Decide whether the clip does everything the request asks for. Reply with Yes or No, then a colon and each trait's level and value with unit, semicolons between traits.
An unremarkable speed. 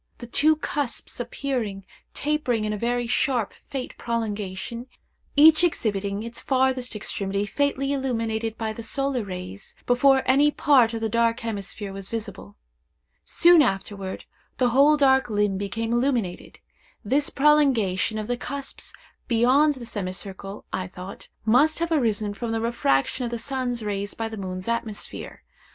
Yes: average, 145 wpm